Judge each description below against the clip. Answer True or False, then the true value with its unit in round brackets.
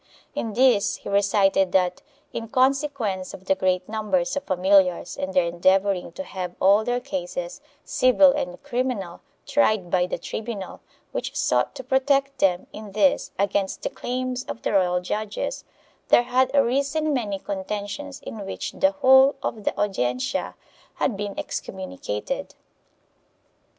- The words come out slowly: False (145 wpm)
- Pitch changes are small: False (5.5 semitones)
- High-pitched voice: True (205 Hz)